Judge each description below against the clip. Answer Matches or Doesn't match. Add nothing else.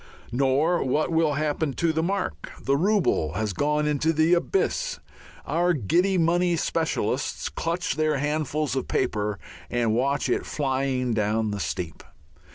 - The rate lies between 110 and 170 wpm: Matches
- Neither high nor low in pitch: Matches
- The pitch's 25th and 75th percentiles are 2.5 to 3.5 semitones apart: Doesn't match